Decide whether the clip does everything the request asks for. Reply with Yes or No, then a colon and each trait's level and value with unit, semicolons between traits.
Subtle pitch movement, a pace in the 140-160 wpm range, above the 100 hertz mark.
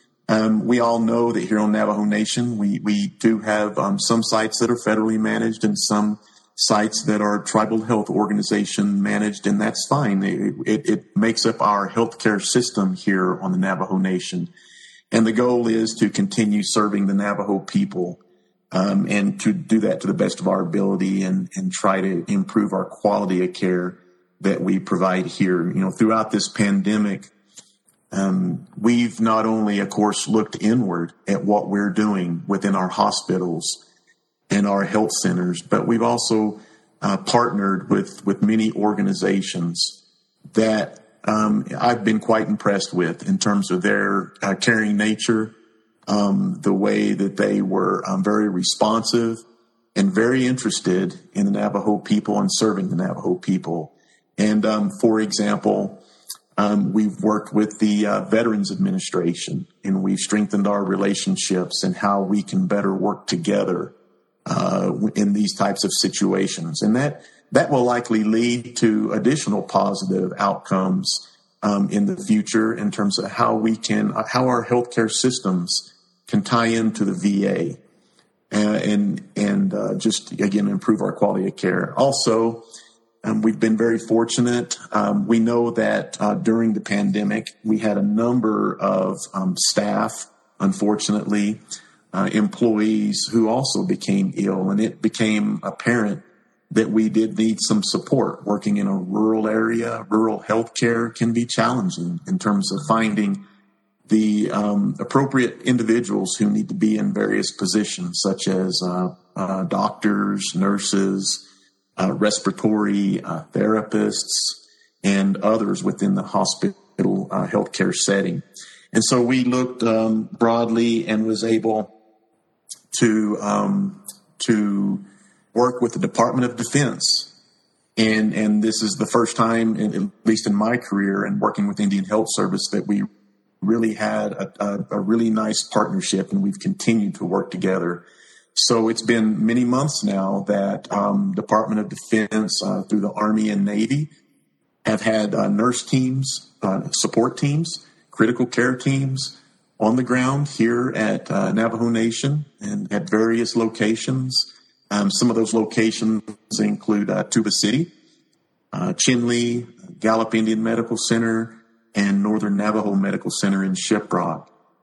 Yes: narrow, 2.3 semitones; average, 150 wpm; low, 110 Hz